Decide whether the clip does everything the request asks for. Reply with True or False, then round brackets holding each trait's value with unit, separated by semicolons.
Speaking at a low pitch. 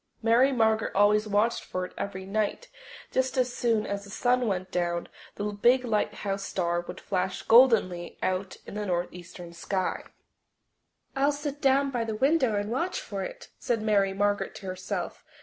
False (210 Hz)